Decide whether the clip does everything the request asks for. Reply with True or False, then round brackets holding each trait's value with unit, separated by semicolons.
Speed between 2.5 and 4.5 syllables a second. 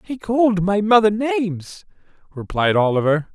False (4.8 syllables/s)